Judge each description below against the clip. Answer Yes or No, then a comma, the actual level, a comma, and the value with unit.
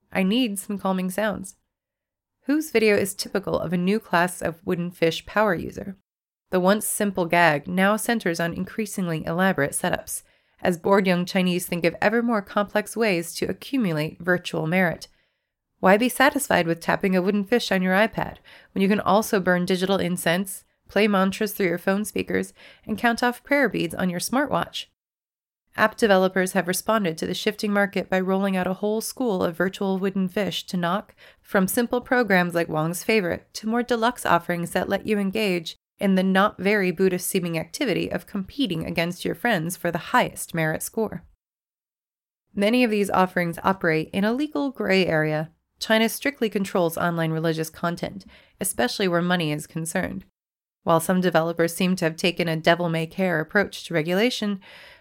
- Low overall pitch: No, high, 190 Hz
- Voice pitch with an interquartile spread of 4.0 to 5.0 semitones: No, average, 3.5 semitones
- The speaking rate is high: No, average, 170 wpm